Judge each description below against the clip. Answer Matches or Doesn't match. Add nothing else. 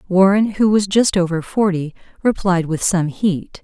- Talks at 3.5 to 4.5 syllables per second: Matches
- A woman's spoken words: Matches